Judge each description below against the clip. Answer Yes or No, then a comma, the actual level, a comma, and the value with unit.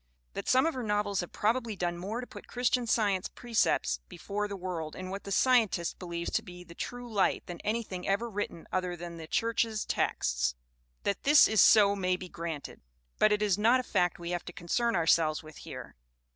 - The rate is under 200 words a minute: No, fast, 205 wpm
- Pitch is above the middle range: Yes, high, 195 Hz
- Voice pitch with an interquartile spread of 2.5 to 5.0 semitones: Yes, average, 4.4 semitones